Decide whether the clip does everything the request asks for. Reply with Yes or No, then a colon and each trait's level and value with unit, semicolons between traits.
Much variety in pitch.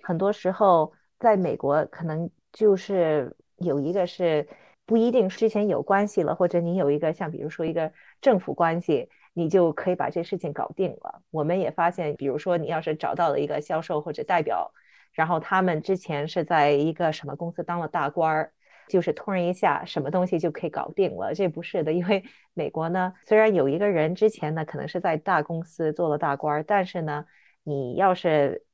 No: average, 3.4 semitones